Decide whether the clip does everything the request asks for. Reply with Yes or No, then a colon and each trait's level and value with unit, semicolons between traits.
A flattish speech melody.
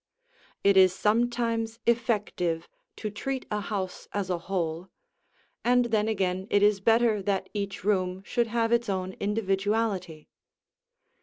No: average, 3.2 semitones